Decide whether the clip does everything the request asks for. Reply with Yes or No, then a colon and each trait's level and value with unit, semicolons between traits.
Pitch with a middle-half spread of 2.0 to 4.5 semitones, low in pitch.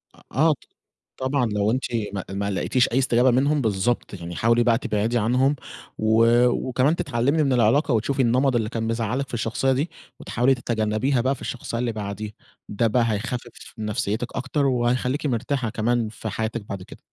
Yes: average, 3.1 semitones; low, 120 Hz